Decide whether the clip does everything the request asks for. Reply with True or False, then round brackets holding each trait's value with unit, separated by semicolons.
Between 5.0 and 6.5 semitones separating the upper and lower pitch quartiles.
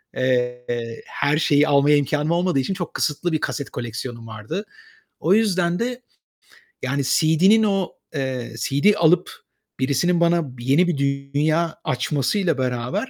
True (5.4 semitones)